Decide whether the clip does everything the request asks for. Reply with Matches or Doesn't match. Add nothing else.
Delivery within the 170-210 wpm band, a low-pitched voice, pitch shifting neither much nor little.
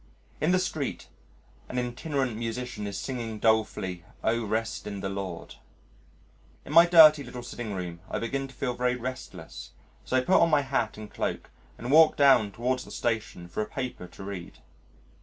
Matches